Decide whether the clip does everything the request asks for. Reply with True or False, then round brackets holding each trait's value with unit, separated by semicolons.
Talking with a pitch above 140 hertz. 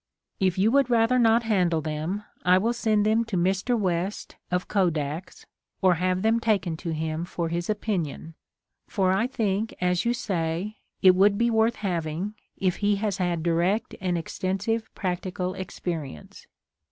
True (190 Hz)